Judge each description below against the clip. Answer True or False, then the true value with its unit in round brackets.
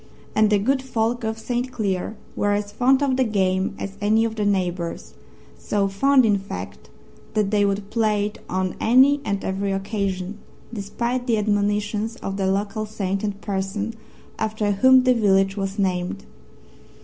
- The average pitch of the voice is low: False (205 Hz)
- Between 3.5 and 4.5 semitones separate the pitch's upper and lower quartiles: False (2.4 semitones)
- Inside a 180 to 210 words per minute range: False (165 wpm)